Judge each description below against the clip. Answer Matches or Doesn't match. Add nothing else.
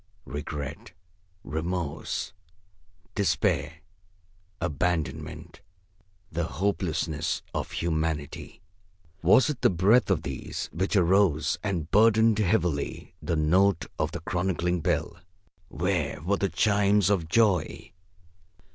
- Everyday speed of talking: Doesn't match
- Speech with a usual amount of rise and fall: Matches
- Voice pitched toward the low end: Matches